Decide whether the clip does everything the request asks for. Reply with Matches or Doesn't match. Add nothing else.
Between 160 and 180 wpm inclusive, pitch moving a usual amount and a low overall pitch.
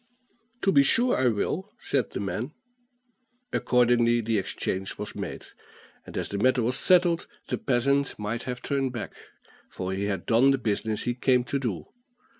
Matches